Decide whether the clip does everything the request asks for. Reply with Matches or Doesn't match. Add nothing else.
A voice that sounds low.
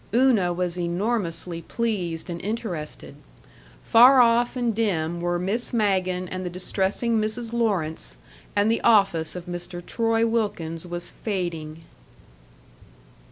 Doesn't match